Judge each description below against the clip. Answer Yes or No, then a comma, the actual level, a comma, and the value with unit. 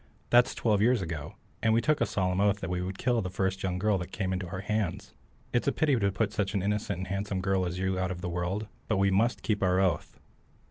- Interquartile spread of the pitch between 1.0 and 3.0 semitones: Yes, narrow, 2.4 semitones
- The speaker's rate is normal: No, fast, 265 wpm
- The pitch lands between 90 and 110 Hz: Yes, very low, 95 Hz